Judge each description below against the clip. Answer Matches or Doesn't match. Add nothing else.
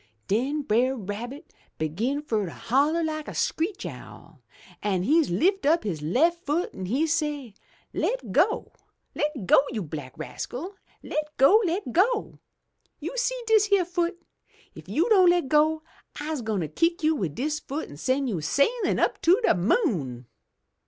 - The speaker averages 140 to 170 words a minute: Matches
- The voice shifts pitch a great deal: Matches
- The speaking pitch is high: Matches